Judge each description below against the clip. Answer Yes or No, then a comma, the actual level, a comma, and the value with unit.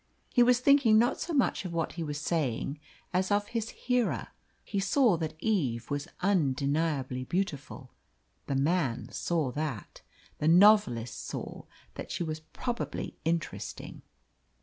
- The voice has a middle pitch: Yes, medium, 165 Hz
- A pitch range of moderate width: No, wide, 6.5 semitones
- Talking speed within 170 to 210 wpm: No, average, 140 wpm